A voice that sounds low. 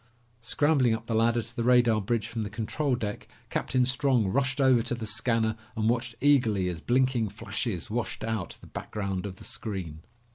Yes: low, 115 Hz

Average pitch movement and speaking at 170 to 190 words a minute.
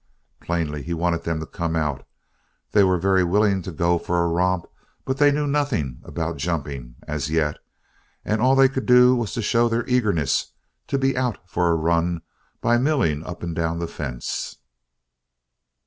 No: wide, 6.5 semitones; average, 180 wpm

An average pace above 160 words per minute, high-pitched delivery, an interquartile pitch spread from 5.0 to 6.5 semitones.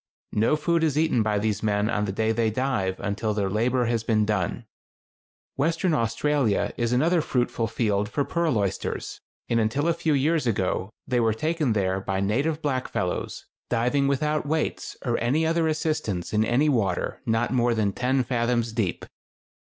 No: average, 170 wpm; low, 120 Hz; wide, 5.5 semitones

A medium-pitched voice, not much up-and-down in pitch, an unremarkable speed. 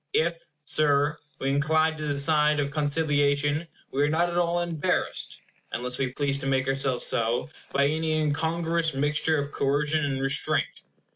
Yes: medium, 145 Hz; narrow, 2.2 semitones; average, 160 wpm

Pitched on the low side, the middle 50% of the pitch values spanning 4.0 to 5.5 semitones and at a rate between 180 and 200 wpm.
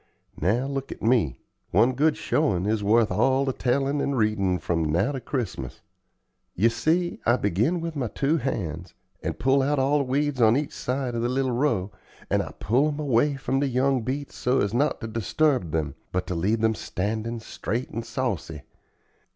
Yes: low, 120 Hz; average, 4.6 semitones; average, 190 wpm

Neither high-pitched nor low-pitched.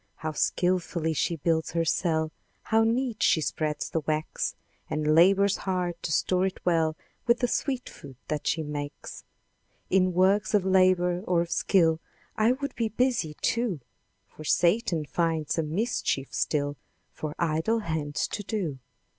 Yes: medium, 170 Hz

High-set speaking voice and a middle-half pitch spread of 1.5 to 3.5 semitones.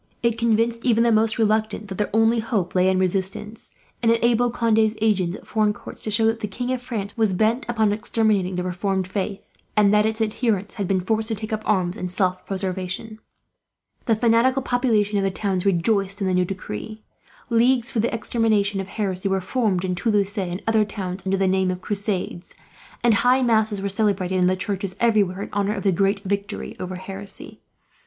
Yes: high, 205 Hz; average, 2.9 semitones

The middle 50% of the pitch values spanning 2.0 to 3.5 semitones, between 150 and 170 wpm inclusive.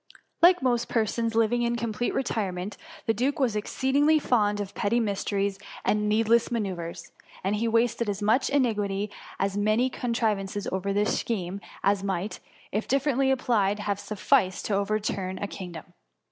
Yes: average, 3.1 semitones; average, 165 wpm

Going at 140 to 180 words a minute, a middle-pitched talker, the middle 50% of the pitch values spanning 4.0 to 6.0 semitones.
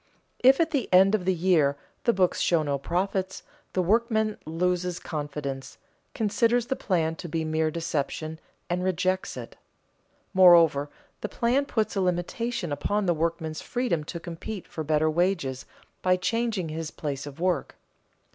Yes: average, 155 wpm; medium, 180 Hz; average, 4.3 semitones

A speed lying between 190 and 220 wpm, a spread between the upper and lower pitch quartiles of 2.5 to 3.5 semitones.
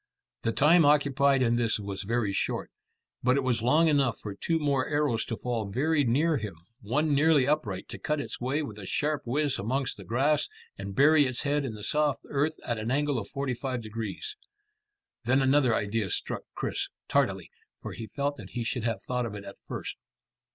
No: average, 200 wpm; average, 4.4 semitones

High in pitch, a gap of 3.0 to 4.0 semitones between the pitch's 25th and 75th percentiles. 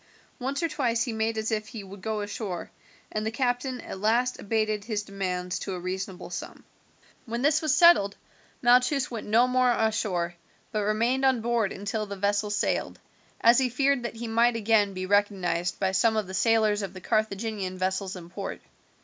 Yes: high, 215 Hz; average, 3.3 semitones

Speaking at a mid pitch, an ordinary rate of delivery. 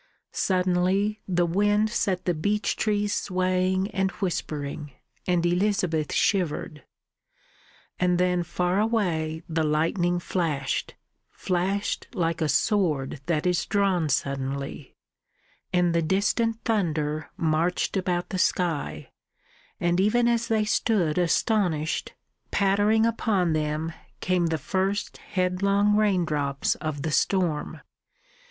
No: medium, 180 Hz; slow, 110 wpm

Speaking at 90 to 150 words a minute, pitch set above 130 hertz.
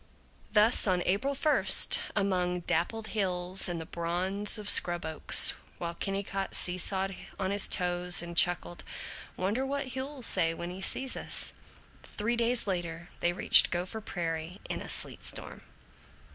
Yes: average, 145 wpm; medium, 185 Hz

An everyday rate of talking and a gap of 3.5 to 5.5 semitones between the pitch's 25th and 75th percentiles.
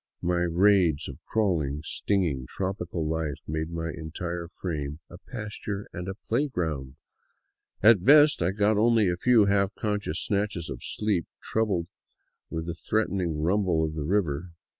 Yes: average, 150 wpm; average, 4.3 semitones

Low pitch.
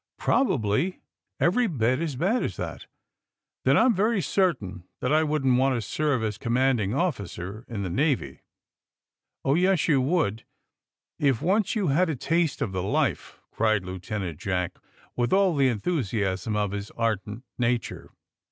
Yes: low, 130 Hz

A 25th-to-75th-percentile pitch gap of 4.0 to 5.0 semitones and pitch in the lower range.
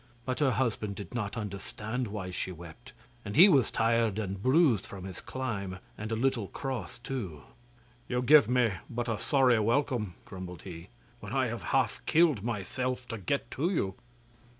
Yes: average, 4.6 semitones; low, 115 Hz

